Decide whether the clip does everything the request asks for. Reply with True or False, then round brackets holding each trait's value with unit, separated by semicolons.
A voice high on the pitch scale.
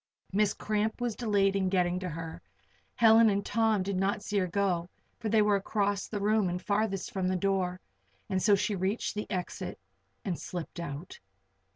True (195 Hz)